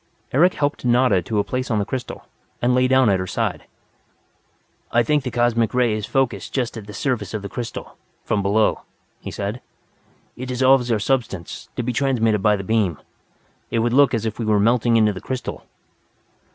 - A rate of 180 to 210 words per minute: Yes, average, 190 wpm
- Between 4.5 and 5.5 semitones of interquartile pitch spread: No, average, 3.2 semitones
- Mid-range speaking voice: No, low, 115 Hz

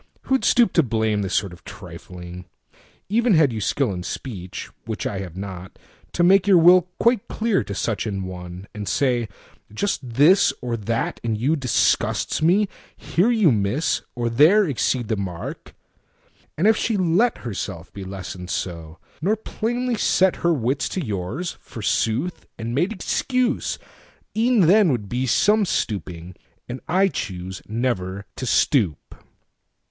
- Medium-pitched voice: No, low, 120 Hz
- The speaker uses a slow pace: Yes, slow, 130 wpm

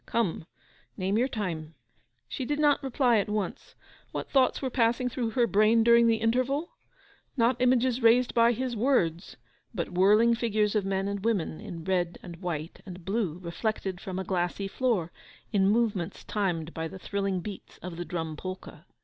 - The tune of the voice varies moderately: Yes, average, 4.5 semitones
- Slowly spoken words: No, average, 175 wpm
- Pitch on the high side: Yes, high, 210 Hz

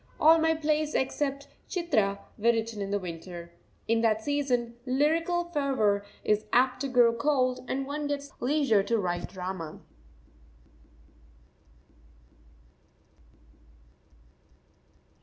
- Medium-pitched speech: No, very high, 255 Hz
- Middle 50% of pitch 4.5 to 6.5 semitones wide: Yes, wide, 5.6 semitones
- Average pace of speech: No, slow, 110 wpm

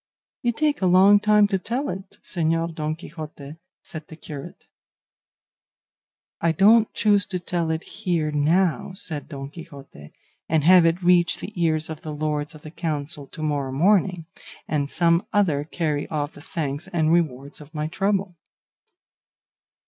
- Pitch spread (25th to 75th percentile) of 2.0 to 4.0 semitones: Yes, average, 3.5 semitones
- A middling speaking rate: Yes, average, 155 wpm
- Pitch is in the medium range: Yes, medium, 165 Hz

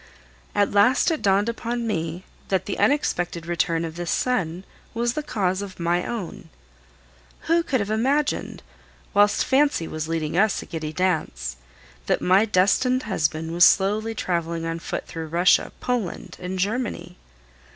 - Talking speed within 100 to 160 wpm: Yes, average, 150 wpm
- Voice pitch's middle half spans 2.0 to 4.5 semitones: No, average, 5.1 semitones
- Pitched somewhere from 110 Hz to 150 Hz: No, medium, 185 Hz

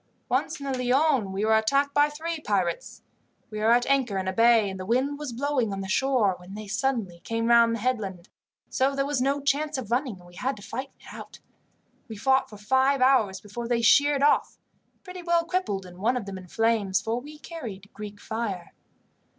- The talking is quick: Yes, fast, 215 wpm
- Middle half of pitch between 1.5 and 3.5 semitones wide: No, average, 5.3 semitones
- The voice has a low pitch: No, high, 235 Hz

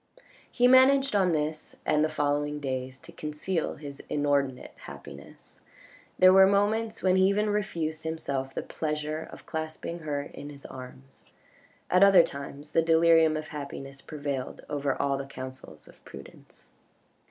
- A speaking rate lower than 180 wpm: Yes, average, 150 wpm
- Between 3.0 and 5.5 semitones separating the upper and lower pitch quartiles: Yes, average, 3.7 semitones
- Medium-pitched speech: Yes, medium, 150 Hz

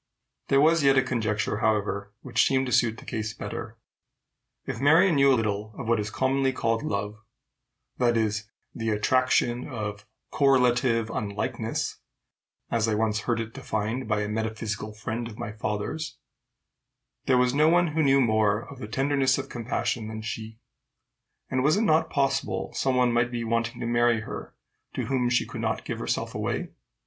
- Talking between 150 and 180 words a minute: Yes, average, 175 wpm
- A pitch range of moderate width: Yes, average, 3.4 semitones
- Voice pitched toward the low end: Yes, low, 115 Hz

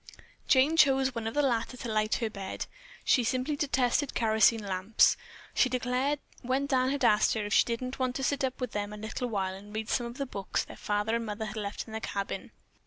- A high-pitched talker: Yes, high, 235 Hz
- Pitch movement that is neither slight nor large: Yes, average, 3.5 semitones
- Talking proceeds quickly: Yes, fast, 230 wpm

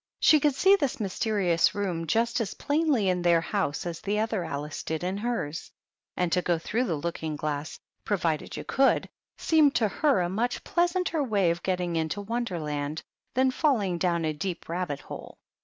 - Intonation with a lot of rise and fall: Yes, wide, 6.3 semitones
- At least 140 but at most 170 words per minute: No, average, 185 wpm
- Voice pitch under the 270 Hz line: Yes, medium, 185 Hz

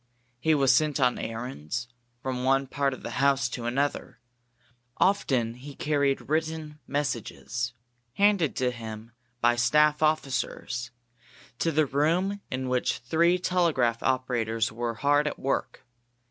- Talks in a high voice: No, low, 135 Hz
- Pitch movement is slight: No, average, 4.0 semitones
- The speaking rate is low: Yes, slow, 130 wpm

